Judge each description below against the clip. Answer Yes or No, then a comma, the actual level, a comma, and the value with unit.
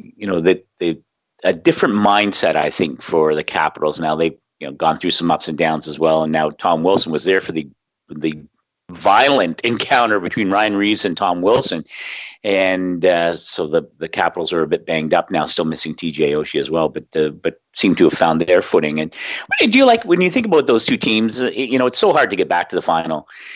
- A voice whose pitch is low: Yes, very low, 85 Hz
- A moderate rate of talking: No, fast, 230 wpm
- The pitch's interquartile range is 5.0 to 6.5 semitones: Yes, wide, 5.4 semitones